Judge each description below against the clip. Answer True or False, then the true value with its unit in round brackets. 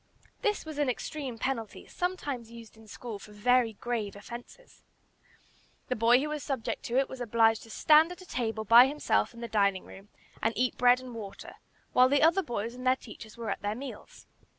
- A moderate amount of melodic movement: True (3.3 semitones)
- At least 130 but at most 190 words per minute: False (200 wpm)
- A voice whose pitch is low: False (240 Hz)